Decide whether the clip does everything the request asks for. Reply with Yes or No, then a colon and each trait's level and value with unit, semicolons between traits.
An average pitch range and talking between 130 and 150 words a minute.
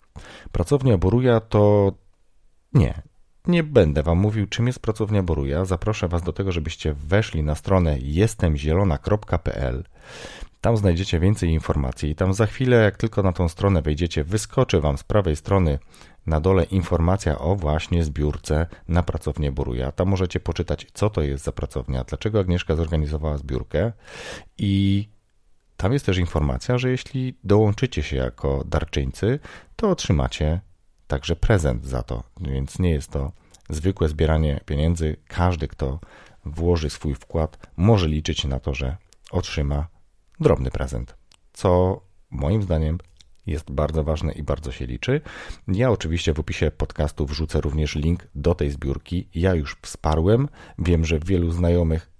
Yes: average, 4.4 semitones; average, 145 wpm